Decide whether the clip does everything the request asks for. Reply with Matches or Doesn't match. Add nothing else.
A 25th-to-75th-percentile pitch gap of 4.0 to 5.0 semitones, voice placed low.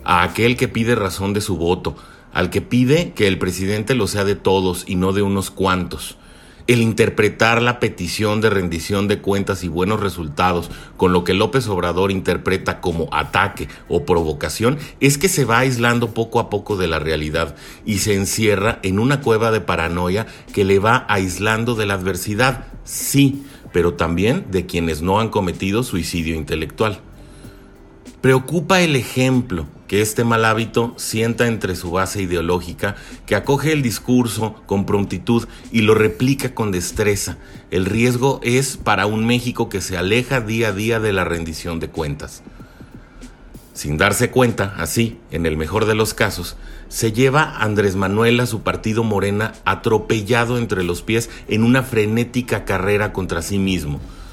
Matches